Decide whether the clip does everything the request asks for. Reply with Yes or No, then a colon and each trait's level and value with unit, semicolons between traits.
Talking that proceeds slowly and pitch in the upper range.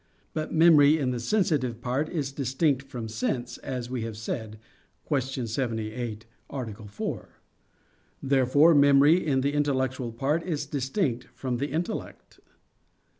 No: slow, 130 wpm; low, 130 Hz